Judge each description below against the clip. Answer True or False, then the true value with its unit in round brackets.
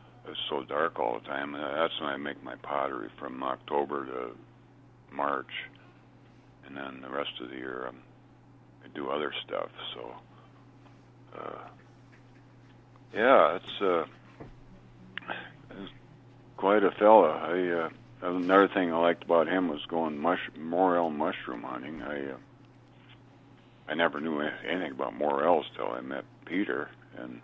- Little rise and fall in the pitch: False (5.3 semitones)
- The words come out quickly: False (140 wpm)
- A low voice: True (80 Hz)